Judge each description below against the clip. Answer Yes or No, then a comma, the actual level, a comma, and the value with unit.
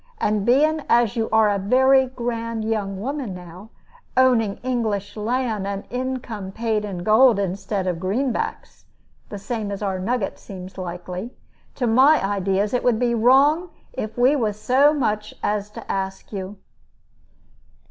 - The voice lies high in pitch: Yes, high, 220 Hz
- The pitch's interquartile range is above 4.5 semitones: No, average, 4.0 semitones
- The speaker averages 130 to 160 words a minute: Yes, average, 150 wpm